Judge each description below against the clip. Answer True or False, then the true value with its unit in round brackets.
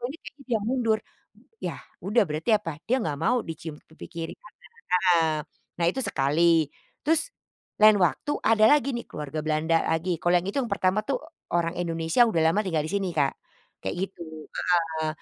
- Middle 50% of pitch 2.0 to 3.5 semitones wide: False (5.2 semitones)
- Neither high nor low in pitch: True (175 Hz)